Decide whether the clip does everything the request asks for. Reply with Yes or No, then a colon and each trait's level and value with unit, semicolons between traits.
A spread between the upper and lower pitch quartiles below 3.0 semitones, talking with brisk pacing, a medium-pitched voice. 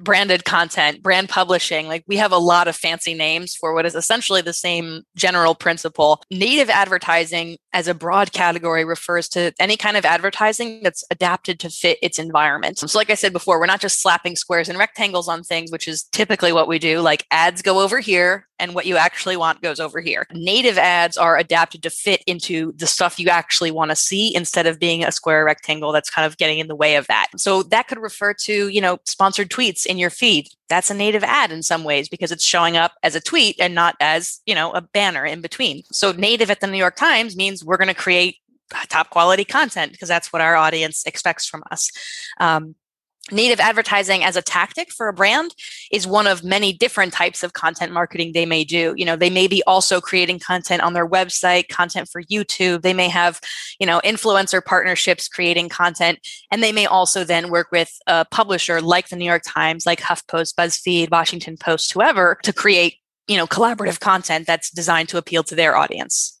Yes: narrow, 2.6 semitones; fast, 210 wpm; medium, 175 Hz